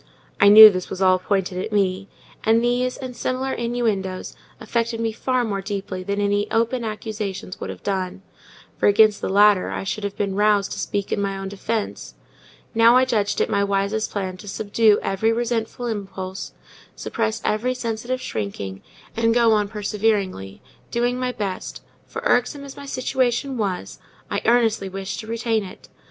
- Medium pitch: No, high, 210 Hz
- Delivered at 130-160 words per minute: No, average, 175 wpm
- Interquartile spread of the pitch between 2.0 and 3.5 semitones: Yes, average, 2.9 semitones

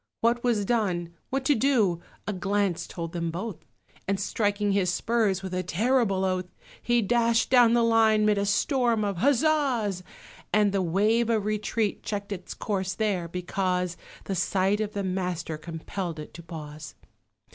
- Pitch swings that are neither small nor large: Yes, average, 3.8 semitones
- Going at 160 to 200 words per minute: Yes, average, 165 wpm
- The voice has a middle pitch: No, high, 200 Hz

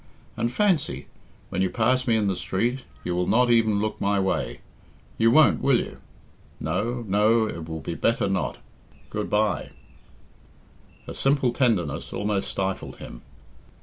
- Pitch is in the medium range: No, low, 110 Hz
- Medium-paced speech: Yes, average, 150 wpm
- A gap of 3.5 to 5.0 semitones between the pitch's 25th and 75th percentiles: Yes, average, 4.1 semitones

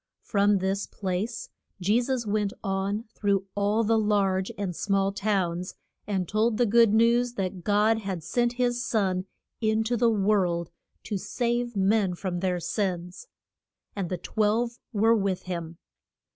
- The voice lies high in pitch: Yes, high, 205 Hz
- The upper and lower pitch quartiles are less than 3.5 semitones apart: Yes, average, 3.0 semitones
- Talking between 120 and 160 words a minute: Yes, average, 150 wpm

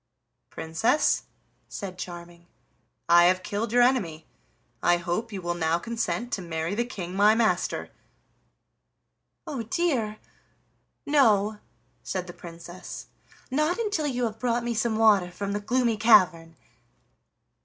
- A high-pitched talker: Yes, high, 210 Hz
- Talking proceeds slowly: Yes, slow, 130 wpm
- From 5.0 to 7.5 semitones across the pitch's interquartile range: Yes, average, 5.3 semitones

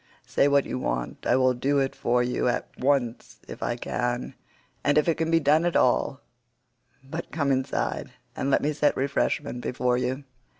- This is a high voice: No, low, 135 Hz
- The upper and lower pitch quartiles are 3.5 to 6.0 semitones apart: No, average, 2.7 semitones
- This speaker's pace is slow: No, average, 185 wpm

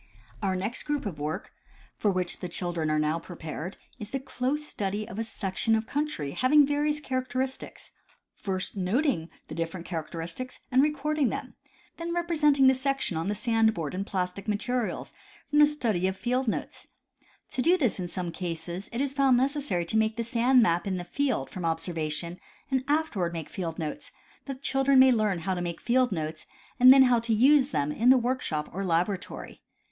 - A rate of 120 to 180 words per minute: No, average, 195 wpm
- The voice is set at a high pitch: Yes, high, 220 Hz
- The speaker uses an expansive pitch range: Yes, wide, 7.1 semitones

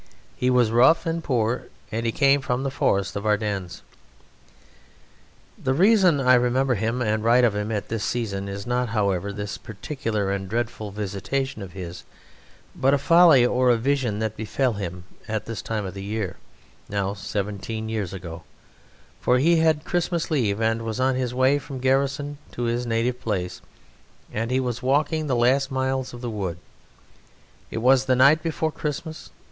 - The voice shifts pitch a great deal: No, average, 4.3 semitones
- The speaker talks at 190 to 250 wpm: No, average, 175 wpm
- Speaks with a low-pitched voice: Yes, low, 120 Hz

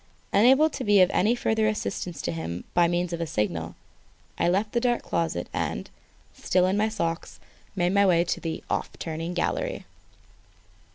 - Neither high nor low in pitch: Yes, medium, 180 Hz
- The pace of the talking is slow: No, average, 175 wpm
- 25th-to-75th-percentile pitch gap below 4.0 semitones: No, average, 4.6 semitones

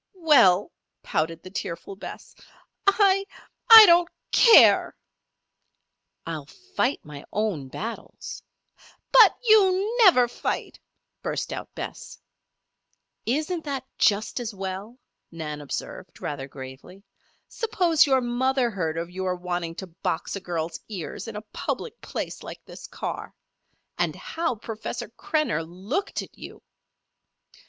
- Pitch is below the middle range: No, high, 215 Hz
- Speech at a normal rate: No, slow, 120 wpm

